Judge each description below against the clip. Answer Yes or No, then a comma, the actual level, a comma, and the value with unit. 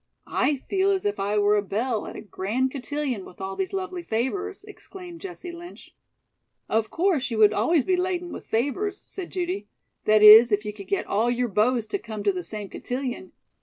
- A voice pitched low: No, very high, 250 Hz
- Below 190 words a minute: No, fast, 205 wpm